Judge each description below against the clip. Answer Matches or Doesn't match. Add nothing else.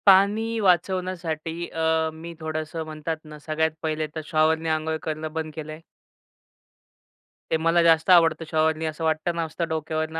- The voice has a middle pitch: Matches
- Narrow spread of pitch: Matches